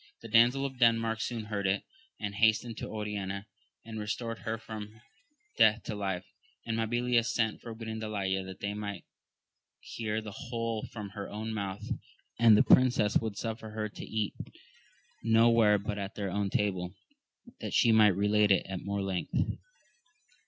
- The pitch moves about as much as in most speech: No, narrow, 1.9 semitones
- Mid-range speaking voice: No, low, 110 Hz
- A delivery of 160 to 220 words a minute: Yes, average, 165 wpm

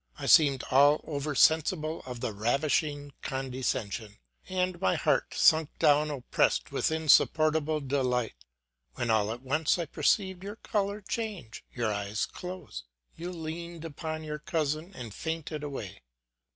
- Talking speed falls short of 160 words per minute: Yes, average, 140 wpm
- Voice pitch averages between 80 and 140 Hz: No, medium, 150 Hz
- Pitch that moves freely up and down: No, average, 4.1 semitones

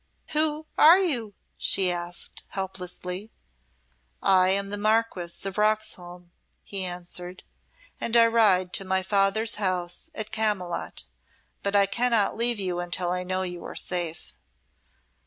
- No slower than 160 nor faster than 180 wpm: No, slow, 135 wpm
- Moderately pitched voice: No, high, 195 Hz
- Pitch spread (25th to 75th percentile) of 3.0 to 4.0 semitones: Yes, average, 3.3 semitones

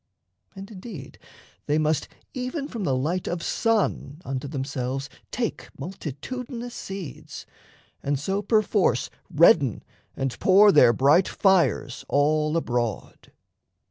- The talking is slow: Yes, slow, 110 wpm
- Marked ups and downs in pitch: Yes, wide, 6.9 semitones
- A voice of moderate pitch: Yes, medium, 160 Hz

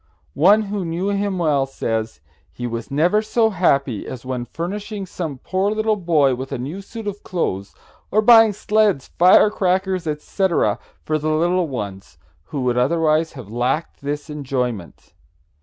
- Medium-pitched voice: Yes, medium, 165 Hz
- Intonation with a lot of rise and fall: Yes, wide, 6.9 semitones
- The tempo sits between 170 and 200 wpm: No, average, 155 wpm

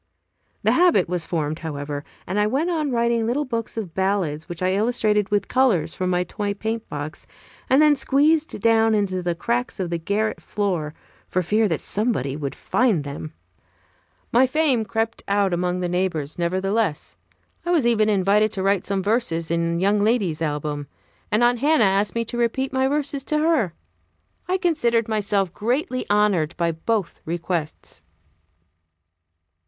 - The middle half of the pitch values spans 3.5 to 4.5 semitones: No, wide, 5.4 semitones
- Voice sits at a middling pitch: No, high, 205 Hz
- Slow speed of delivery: No, average, 160 wpm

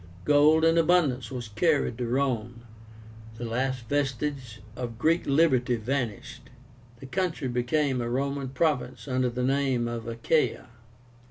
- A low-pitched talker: Yes, low, 130 Hz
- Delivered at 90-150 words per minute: Yes, slow, 135 wpm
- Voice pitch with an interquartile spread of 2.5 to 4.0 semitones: Yes, average, 3.2 semitones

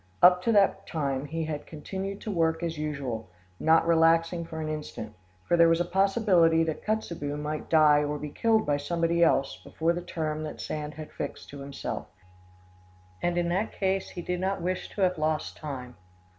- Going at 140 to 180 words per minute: No, average, 190 wpm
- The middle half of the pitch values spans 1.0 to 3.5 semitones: Yes, average, 2.8 semitones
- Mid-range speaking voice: Yes, medium, 165 Hz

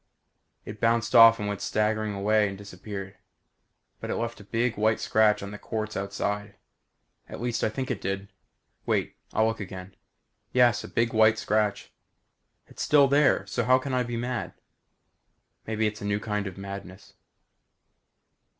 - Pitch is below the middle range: Yes, low, 110 Hz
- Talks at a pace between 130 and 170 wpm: Yes, average, 165 wpm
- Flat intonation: Yes, narrow, 2.3 semitones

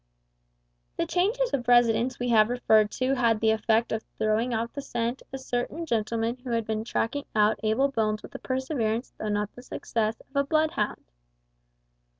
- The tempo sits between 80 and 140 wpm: No, average, 175 wpm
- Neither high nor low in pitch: No, high, 235 Hz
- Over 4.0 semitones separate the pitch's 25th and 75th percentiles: No, average, 3.0 semitones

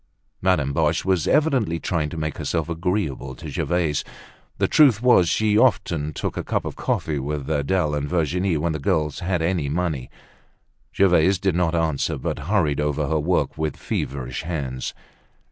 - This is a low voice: Yes, very low, 80 Hz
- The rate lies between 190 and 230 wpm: No, average, 165 wpm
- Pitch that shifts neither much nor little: Yes, average, 3.6 semitones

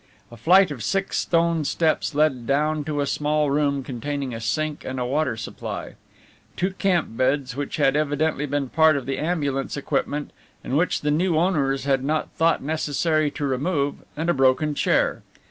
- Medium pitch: Yes, medium, 145 Hz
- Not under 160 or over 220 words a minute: Yes, average, 180 wpm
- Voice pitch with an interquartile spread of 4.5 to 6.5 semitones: No, narrow, 2.5 semitones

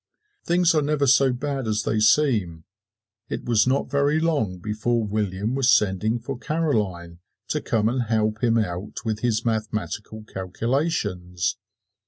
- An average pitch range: Yes, average, 4.4 semitones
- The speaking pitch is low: Yes, low, 110 Hz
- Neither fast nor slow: Yes, average, 145 wpm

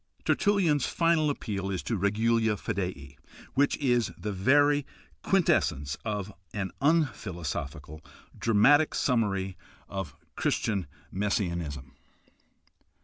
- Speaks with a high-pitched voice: No, low, 105 Hz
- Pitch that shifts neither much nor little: No, wide, 6.9 semitones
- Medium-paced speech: No, slow, 100 wpm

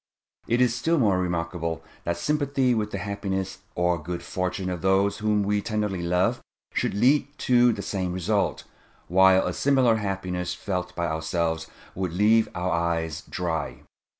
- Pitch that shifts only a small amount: No, average, 3.5 semitones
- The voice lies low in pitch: Yes, very low, 95 Hz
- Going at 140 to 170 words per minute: Yes, average, 155 wpm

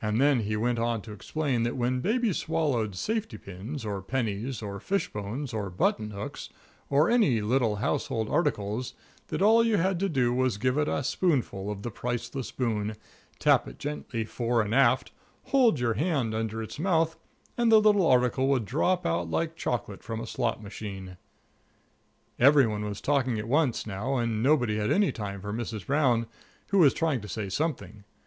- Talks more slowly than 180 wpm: No, average, 185 wpm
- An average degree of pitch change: No, wide, 5.7 semitones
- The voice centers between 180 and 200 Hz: No, low, 120 Hz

